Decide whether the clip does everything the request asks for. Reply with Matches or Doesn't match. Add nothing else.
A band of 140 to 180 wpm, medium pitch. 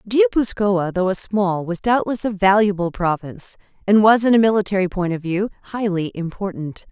Doesn't match